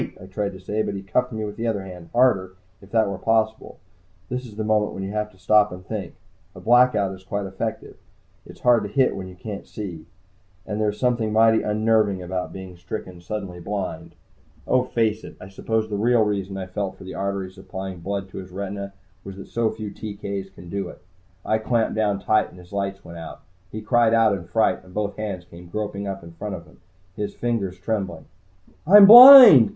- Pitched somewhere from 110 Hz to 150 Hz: No, low, 100 Hz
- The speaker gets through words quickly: Yes, fast, 215 wpm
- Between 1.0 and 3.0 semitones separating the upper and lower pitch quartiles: Yes, narrow, 2.6 semitones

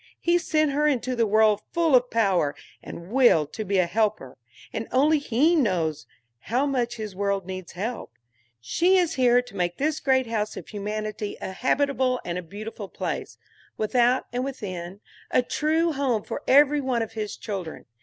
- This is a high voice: Yes, high, 230 Hz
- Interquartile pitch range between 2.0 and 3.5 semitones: No, average, 5.2 semitones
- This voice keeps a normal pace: Yes, average, 175 wpm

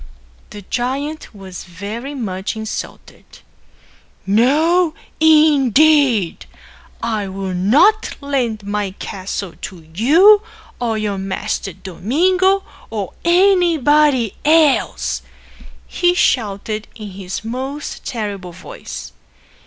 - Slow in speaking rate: Yes, slow, 90 wpm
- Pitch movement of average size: No, wide, 7.6 semitones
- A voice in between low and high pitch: No, high, 230 Hz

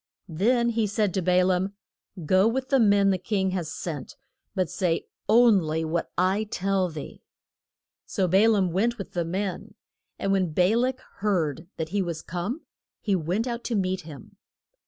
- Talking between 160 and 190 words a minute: Yes, average, 180 wpm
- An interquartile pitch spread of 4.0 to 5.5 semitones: No, average, 3.4 semitones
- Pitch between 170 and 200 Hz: Yes, high, 190 Hz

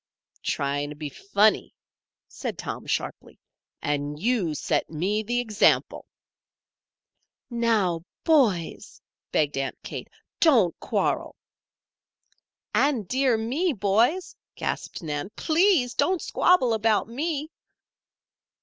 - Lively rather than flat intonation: Yes, wide, 8.3 semitones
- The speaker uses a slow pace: Yes, slow, 100 wpm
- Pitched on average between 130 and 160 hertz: No, high, 220 Hz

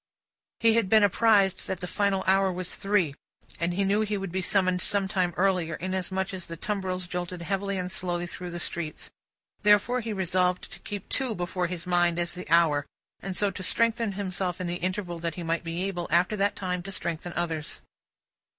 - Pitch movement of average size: No, narrow, 2.2 semitones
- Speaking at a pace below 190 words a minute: No, average, 200 wpm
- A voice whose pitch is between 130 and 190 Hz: Yes, medium, 185 Hz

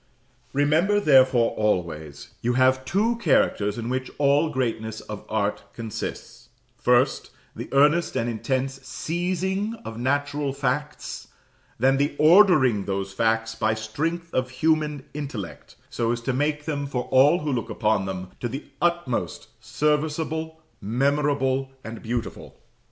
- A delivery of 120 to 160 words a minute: Yes, slow, 135 wpm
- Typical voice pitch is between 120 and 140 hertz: Yes, low, 135 Hz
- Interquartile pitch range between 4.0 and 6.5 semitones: Yes, average, 4.7 semitones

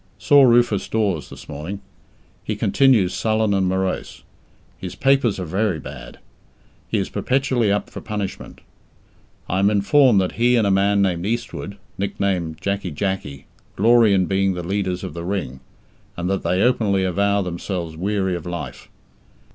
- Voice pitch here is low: Yes, low, 100 Hz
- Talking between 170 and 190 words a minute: No, average, 155 wpm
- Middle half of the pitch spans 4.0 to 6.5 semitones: No, average, 3.0 semitones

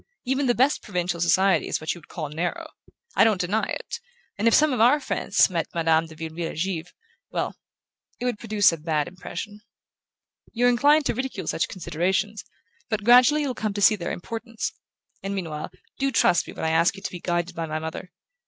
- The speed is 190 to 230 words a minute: Yes, fast, 205 wpm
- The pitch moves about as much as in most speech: No, wide, 5.8 semitones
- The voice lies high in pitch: Yes, high, 195 Hz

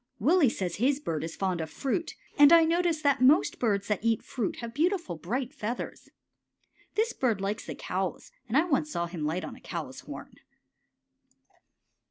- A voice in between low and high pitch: No, high, 240 Hz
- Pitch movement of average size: No, wide, 7.9 semitones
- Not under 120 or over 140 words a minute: No, average, 180 wpm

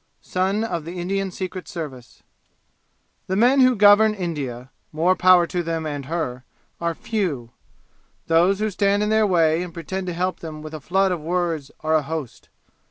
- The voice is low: No, medium, 175 Hz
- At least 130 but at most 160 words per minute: No, average, 175 wpm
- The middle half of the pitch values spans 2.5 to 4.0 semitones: Yes, average, 3.5 semitones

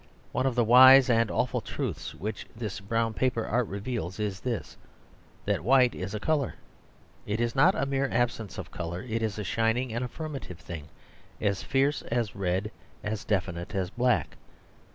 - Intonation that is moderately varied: Yes, average, 4.1 semitones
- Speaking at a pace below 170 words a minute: No, average, 175 wpm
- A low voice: Yes, low, 115 Hz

